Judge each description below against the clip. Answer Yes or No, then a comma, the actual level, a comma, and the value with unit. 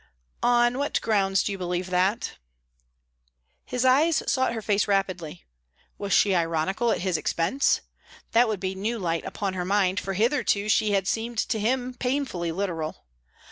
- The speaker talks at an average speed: Yes, average, 160 wpm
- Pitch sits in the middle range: No, high, 200 Hz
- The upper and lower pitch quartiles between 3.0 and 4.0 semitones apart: No, average, 4.6 semitones